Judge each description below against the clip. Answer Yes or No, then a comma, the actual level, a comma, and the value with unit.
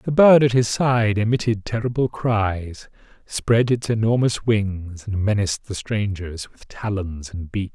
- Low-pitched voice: Yes, low, 110 Hz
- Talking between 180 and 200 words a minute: No, average, 155 wpm